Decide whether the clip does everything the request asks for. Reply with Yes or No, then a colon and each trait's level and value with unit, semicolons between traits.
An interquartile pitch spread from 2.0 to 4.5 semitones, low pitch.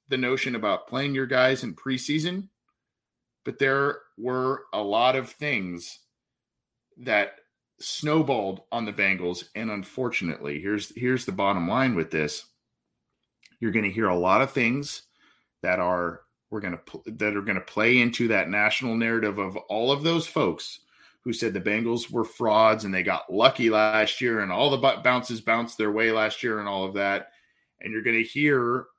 Yes: average, 4.1 semitones; low, 115 Hz